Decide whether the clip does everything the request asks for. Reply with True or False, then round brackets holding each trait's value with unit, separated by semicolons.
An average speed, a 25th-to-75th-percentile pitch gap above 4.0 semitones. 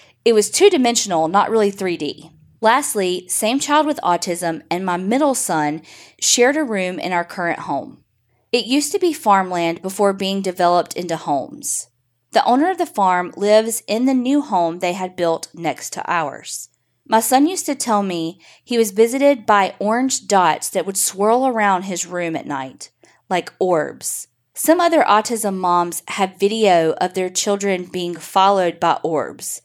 True (170 wpm; 5.0 semitones)